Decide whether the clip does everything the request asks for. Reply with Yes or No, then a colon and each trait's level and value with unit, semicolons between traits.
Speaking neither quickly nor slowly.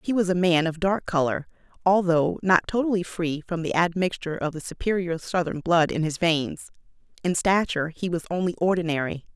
Yes: average, 180 wpm